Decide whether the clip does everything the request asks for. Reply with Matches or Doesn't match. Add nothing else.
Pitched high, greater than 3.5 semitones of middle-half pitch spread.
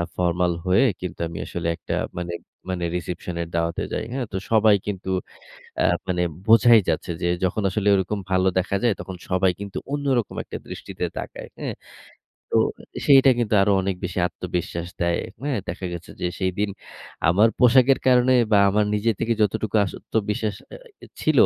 Doesn't match